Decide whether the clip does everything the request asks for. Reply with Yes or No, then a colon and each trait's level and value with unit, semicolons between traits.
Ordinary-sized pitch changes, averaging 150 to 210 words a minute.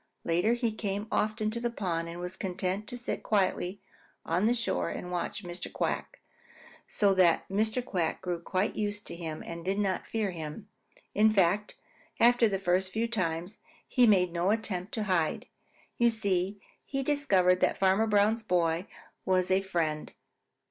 Yes: average, 3.5 semitones; average, 175 wpm